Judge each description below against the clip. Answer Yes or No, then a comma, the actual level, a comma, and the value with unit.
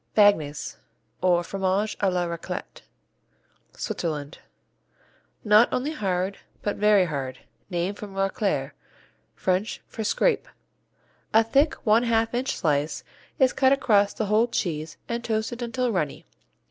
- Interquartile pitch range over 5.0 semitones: No, average, 4.5 semitones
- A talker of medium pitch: No, high, 205 Hz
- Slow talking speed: Yes, slow, 125 wpm